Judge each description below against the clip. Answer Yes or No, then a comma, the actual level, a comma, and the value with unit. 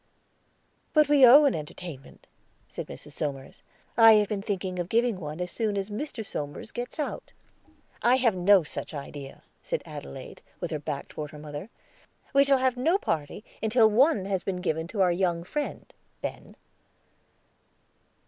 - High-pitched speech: Yes, high, 195 Hz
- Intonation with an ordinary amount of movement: No, wide, 7.5 semitones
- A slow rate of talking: No, average, 165 wpm